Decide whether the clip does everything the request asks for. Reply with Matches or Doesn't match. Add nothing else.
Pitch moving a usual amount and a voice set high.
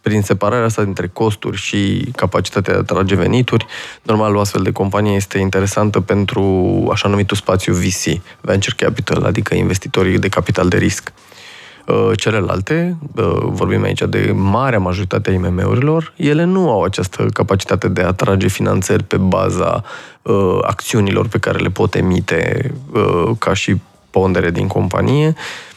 Doesn't match